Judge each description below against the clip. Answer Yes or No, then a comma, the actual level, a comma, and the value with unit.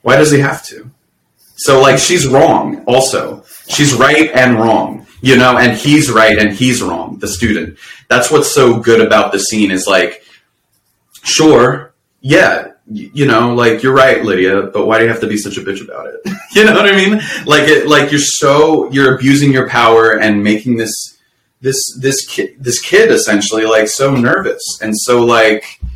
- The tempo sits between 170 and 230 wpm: Yes, average, 190 wpm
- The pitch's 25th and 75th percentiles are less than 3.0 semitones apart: No, average, 4.4 semitones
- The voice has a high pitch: No, low, 125 Hz